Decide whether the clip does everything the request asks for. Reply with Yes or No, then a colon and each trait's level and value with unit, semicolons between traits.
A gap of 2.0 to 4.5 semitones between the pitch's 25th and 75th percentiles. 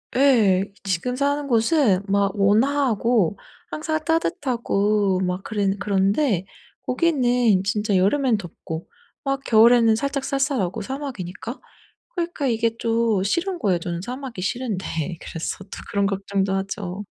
No: wide, 5.6 semitones